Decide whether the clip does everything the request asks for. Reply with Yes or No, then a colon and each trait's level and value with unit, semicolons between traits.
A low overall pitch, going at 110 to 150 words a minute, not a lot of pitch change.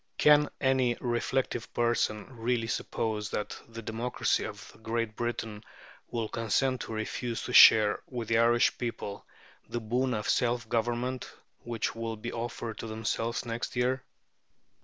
Yes: low, 115 Hz; average, 140 wpm; narrow, 1.6 semitones